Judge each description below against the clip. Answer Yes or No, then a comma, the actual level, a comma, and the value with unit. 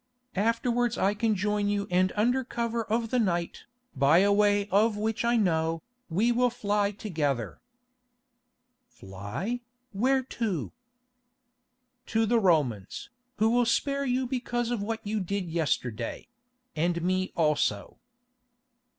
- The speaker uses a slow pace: Yes, slow, 125 wpm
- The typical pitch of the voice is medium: No, high, 205 Hz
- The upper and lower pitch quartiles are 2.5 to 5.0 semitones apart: No, wide, 5.4 semitones